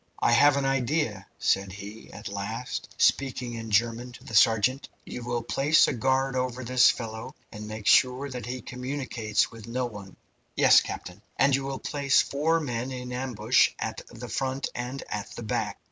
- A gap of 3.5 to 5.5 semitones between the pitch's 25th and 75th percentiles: No, average, 3.1 semitones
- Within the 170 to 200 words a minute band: Yes, average, 180 wpm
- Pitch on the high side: No, low, 125 Hz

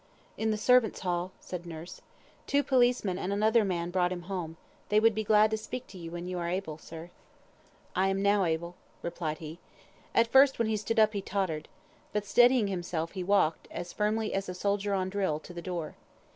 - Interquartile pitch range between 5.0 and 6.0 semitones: No, average, 3.6 semitones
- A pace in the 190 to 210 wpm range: Yes, fast, 205 wpm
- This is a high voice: Yes, high, 195 Hz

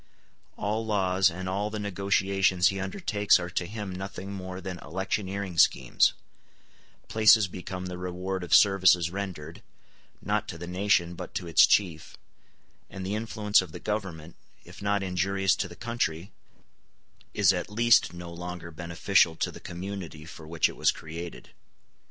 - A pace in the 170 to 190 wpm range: No, average, 155 wpm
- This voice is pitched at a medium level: No, very low, 95 Hz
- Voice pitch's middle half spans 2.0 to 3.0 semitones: Yes, narrow, 2.4 semitones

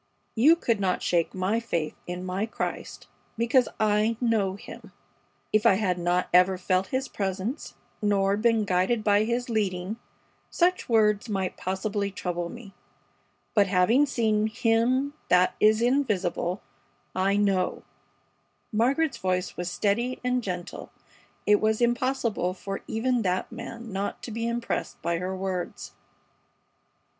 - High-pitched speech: Yes, high, 210 Hz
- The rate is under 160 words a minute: Yes, slow, 135 wpm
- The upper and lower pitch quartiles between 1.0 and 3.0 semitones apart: No, average, 3.8 semitones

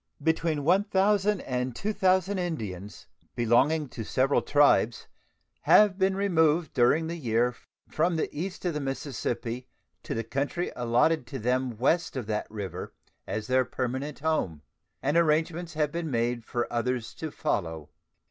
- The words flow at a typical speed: Yes, average, 145 wpm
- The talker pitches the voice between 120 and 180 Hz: Yes, medium, 140 Hz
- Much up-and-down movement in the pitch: Yes, wide, 5.8 semitones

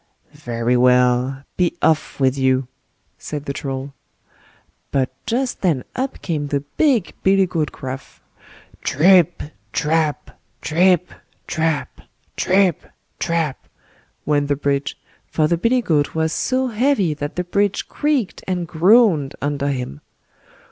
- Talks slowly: Yes, slow, 125 wpm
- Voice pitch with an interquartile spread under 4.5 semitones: No, average, 5.1 semitones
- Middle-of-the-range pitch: Yes, medium, 155 Hz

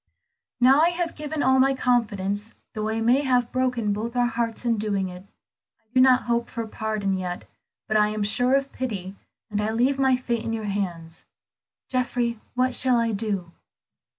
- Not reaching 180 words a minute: No, average, 185 wpm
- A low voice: No, high, 230 Hz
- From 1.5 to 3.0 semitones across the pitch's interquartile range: No, average, 3.5 semitones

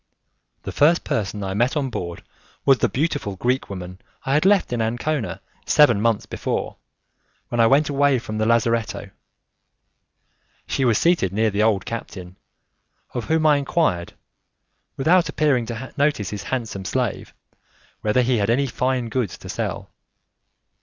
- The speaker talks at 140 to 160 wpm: Yes, average, 155 wpm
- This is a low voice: Yes, low, 120 Hz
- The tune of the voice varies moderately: Yes, average, 5.0 semitones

